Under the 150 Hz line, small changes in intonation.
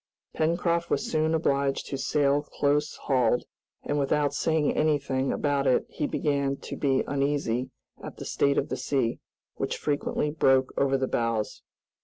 Yes: medium, 140 Hz; narrow, 1.8 semitones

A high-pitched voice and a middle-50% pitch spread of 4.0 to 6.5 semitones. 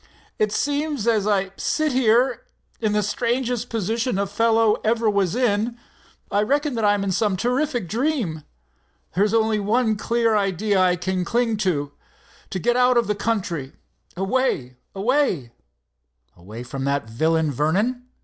Yes: high, 215 Hz; average, 4.4 semitones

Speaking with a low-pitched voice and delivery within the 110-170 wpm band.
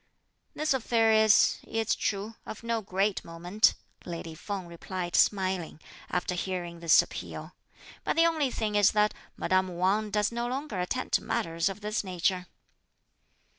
No: high, 200 Hz; average, 150 wpm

